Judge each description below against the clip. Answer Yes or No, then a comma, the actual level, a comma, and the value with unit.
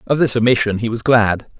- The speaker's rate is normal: No, fast, 225 wpm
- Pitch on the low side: Yes, low, 115 Hz